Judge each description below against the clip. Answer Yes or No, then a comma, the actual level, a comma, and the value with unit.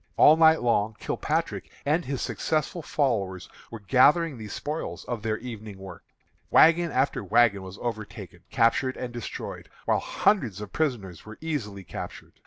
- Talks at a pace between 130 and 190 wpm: Yes, average, 150 wpm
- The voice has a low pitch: Yes, low, 120 Hz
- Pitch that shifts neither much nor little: No, wide, 6.2 semitones